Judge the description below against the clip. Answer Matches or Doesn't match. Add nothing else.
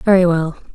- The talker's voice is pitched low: Doesn't match